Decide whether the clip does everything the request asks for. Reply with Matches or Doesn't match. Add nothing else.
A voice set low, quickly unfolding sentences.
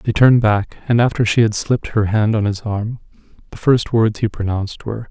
Matches